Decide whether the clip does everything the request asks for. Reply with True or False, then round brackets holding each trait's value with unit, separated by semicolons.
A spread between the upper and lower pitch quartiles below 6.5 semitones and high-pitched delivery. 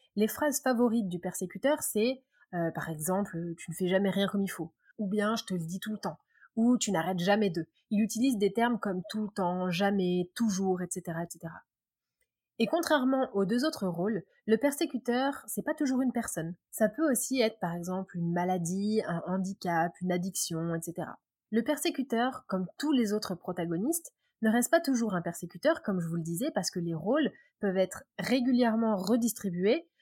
True (5.1 semitones; 205 Hz)